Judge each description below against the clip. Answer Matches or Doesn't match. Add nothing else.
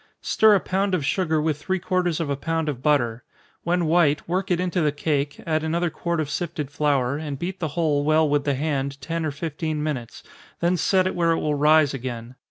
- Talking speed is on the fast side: Matches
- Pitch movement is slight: Doesn't match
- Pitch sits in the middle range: Matches